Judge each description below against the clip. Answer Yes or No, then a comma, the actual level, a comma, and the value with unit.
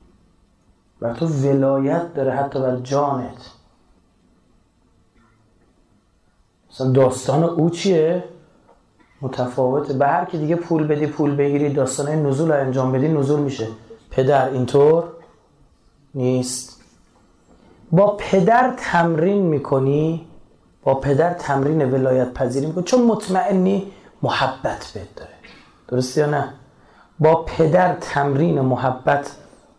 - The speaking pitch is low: No, medium, 145 Hz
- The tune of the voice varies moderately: Yes, average, 4.1 semitones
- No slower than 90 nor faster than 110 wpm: Yes, slow, 105 wpm